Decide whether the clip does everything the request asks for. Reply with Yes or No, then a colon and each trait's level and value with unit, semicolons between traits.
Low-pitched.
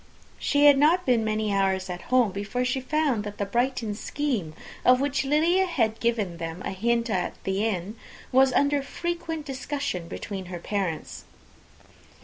No: high, 235 Hz